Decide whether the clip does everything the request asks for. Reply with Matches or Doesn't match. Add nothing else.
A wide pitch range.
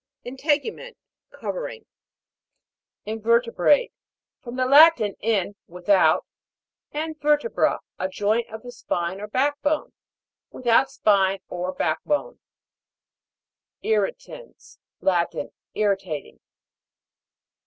Matches